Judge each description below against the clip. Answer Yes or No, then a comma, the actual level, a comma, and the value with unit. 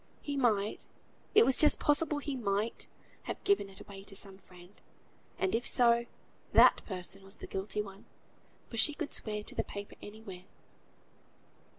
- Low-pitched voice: No, high, 210 Hz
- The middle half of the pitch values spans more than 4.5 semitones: No, average, 4.2 semitones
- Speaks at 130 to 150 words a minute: No, average, 165 wpm